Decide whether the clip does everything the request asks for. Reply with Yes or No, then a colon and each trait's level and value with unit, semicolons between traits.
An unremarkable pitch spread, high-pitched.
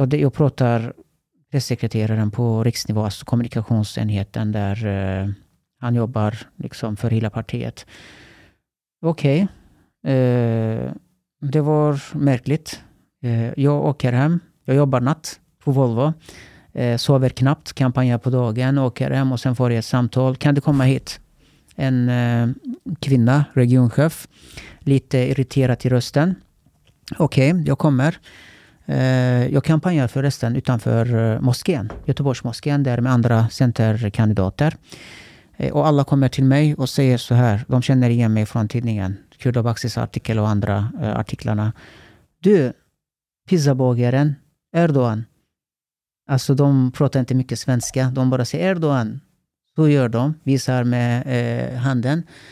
No: average, 3.3 semitones; low, 130 Hz